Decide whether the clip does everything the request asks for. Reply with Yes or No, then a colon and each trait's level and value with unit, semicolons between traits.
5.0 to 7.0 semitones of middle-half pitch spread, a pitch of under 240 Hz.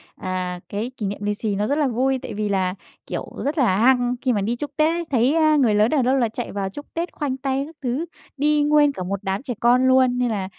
No: wide, 5.4 semitones; very high, 250 Hz